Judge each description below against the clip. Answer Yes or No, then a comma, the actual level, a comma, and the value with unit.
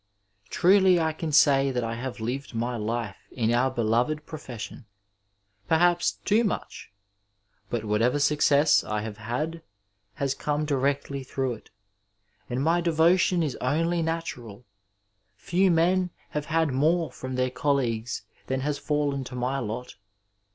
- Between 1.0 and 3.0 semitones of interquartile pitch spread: No, average, 5.0 semitones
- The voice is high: No, medium, 140 Hz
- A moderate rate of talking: Yes, average, 145 wpm